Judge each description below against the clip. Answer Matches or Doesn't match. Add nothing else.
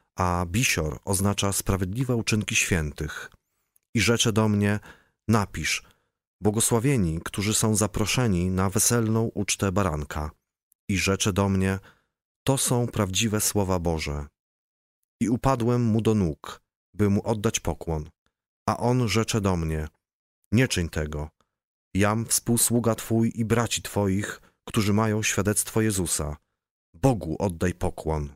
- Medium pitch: Doesn't match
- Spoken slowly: Doesn't match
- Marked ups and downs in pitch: Doesn't match